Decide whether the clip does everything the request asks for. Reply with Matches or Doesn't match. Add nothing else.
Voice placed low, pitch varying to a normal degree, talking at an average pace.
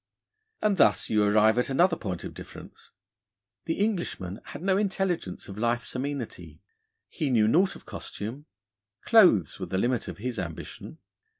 Doesn't match